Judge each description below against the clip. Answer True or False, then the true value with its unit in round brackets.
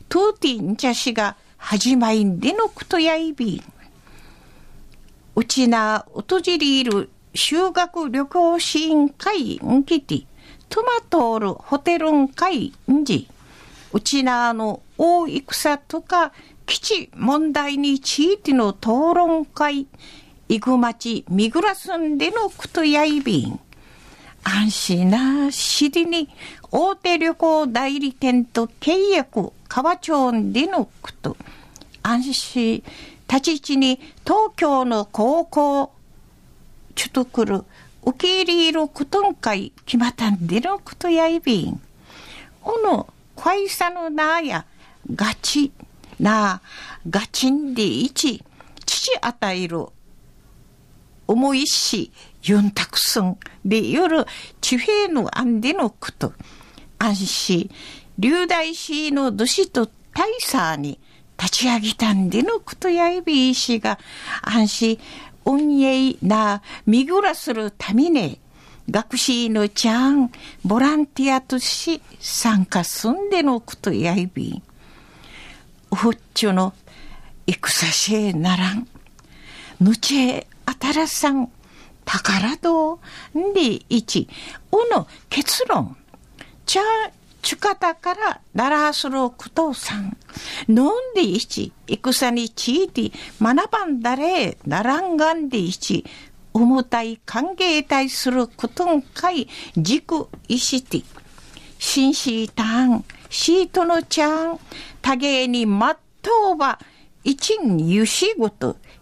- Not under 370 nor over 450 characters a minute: False (205 characters per minute)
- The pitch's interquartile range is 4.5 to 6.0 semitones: False (6.5 semitones)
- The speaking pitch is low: False (270 Hz)